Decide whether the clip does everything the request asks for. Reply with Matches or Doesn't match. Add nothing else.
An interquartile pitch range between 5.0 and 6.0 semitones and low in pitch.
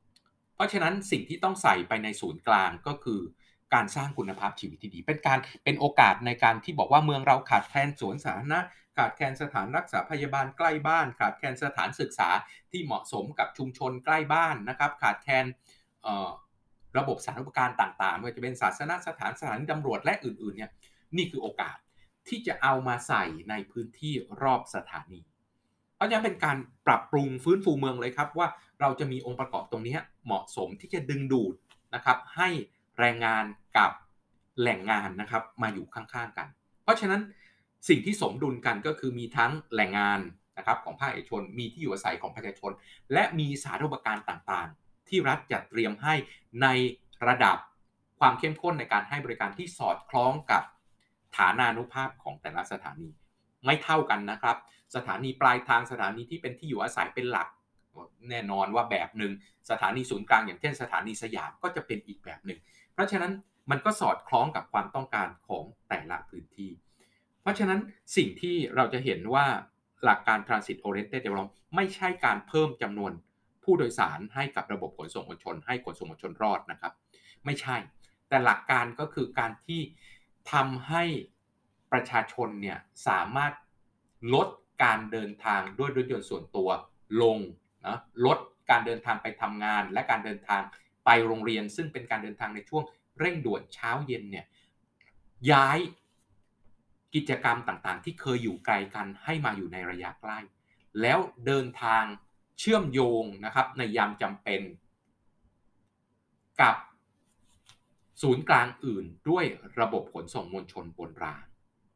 Matches